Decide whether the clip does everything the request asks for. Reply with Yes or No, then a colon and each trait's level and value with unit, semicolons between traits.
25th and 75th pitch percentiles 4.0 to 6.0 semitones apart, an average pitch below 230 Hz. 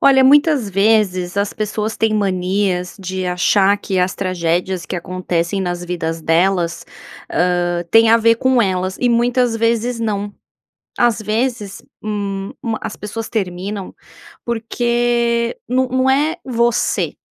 Yes: average, 4.3 semitones; high, 205 Hz